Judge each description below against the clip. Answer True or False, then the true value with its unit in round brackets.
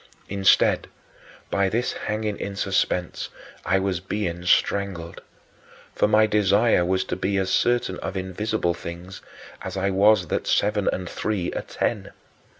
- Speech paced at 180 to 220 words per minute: False (145 wpm)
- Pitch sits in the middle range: False (95 Hz)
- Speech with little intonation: True (2.2 semitones)